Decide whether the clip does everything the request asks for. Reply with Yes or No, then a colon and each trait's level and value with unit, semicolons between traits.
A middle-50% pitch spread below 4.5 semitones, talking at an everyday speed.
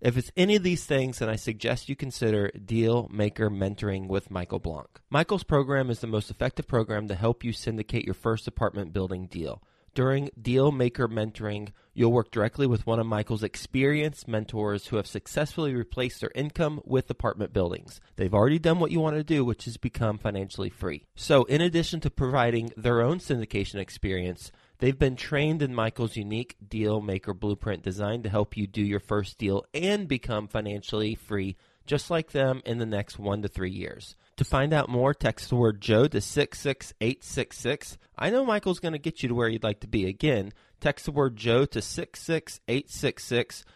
No: average, 4.9 semitones; average, 190 wpm